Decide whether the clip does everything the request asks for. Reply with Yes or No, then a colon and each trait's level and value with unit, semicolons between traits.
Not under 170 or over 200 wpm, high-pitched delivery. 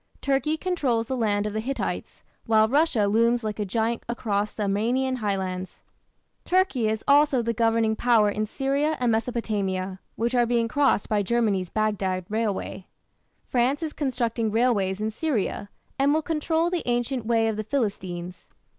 No: average, 160 wpm; high, 230 Hz